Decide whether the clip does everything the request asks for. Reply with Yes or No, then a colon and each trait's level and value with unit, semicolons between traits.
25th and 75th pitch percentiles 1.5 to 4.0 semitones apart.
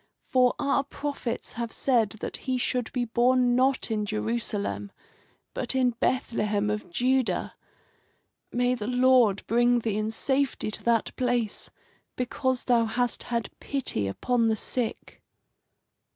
Yes: average, 2.7 semitones